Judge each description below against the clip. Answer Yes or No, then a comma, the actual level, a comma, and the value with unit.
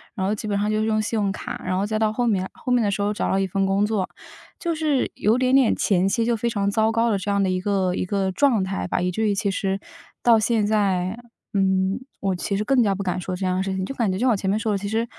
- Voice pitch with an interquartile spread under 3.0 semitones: Yes, narrow, 2.5 semitones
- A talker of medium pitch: No, high, 205 Hz